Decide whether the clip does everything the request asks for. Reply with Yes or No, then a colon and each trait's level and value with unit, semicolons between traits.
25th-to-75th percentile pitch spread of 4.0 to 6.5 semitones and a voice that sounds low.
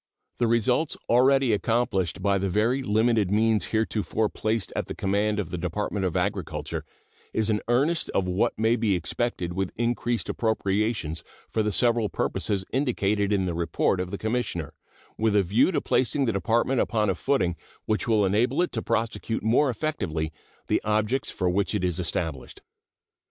No: average, 3.6 semitones; low, 110 Hz